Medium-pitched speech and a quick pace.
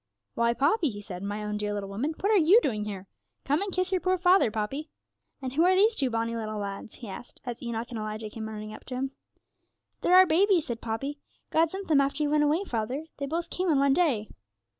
No: very high, 270 Hz; fast, 240 wpm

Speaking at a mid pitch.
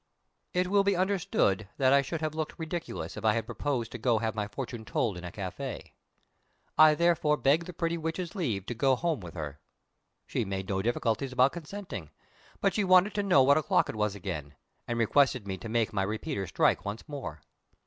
No: low, 125 Hz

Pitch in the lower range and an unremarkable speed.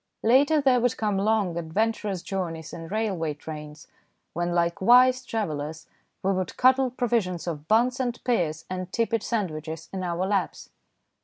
No: high, 190 Hz; average, 150 wpm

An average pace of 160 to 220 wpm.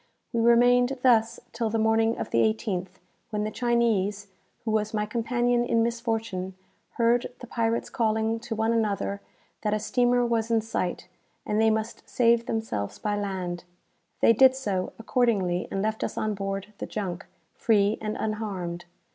Yes: average, 165 wpm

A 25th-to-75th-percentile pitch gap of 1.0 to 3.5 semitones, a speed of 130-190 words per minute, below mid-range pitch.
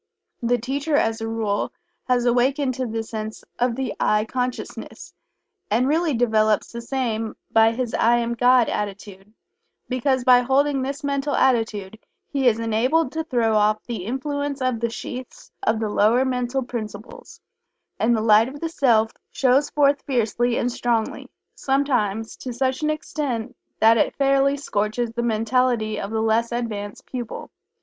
No: average, 3.1 semitones; average, 160 wpm; high, 240 Hz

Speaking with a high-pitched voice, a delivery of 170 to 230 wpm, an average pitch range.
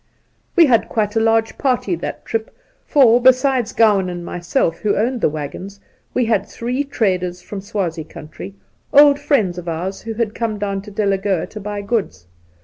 Yes: high, 210 Hz; average, 180 wpm; average, 3.8 semitones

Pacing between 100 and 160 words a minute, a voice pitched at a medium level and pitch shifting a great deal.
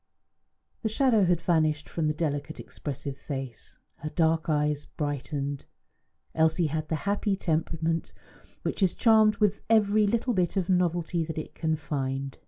No: average, 155 wpm; medium, 160 Hz; average, 4.2 semitones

